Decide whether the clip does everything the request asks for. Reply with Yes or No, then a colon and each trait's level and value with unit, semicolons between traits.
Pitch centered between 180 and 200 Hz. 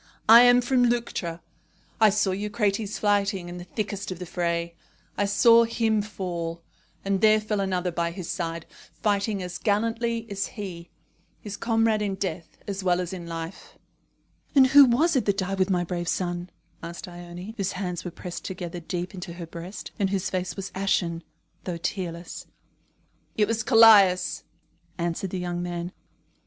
Yes: high, 190 Hz